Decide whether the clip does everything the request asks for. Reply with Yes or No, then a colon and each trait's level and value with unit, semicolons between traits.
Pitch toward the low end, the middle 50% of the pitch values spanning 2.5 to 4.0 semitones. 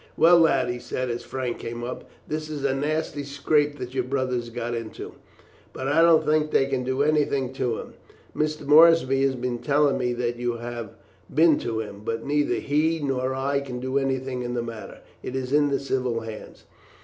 Yes: low, 130 Hz; average, 3.1 semitones